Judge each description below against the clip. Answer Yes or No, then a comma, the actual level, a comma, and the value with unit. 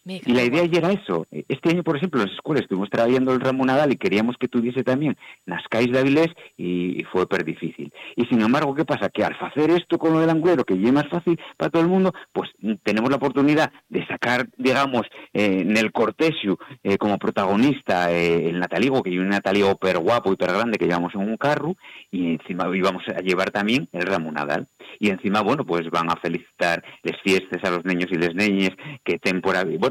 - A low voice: Yes, low, 110 Hz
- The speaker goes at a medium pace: No, fast, 225 wpm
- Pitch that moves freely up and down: Yes, wide, 7.6 semitones